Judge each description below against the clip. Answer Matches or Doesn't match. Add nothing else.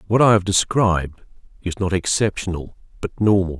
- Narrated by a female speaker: Doesn't match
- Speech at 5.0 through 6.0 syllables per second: Matches